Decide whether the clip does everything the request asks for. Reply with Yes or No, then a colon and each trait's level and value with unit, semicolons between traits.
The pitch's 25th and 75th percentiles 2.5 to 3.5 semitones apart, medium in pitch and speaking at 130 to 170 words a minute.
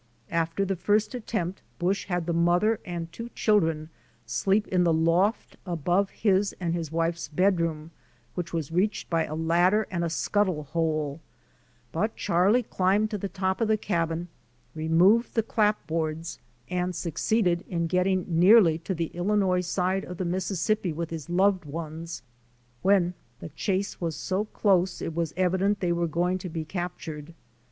Yes: average, 2.9 semitones; medium, 175 Hz; average, 160 wpm